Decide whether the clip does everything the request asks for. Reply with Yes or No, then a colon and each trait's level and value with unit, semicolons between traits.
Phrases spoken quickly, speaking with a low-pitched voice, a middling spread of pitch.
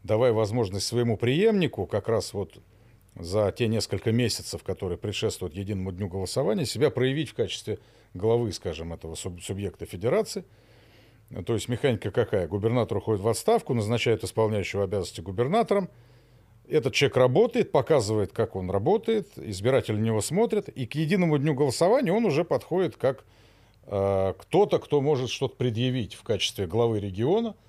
No: average, 145 wpm; low, 115 Hz; average, 4.1 semitones